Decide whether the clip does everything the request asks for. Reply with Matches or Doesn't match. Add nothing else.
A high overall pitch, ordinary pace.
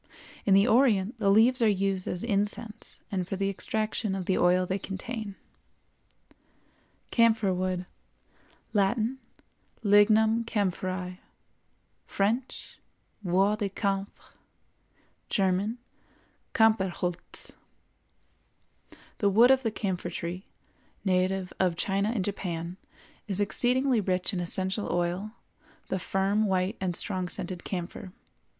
Doesn't match